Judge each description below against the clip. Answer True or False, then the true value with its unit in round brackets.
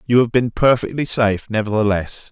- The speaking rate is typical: True (155 wpm)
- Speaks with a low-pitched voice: True (115 Hz)